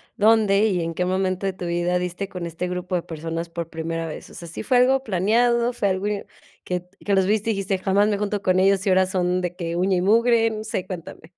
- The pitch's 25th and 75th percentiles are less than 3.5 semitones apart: Yes, average, 2.7 semitones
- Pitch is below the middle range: No, medium, 185 Hz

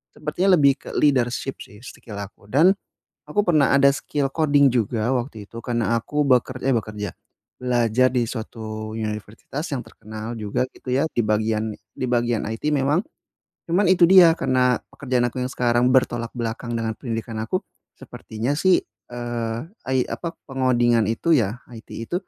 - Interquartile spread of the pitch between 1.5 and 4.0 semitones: Yes, average, 3.6 semitones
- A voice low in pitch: Yes, low, 120 Hz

